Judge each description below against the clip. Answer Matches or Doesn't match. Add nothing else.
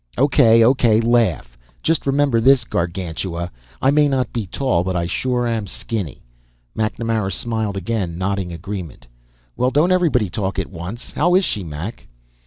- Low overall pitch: Matches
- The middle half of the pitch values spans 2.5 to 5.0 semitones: Doesn't match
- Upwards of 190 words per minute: Doesn't match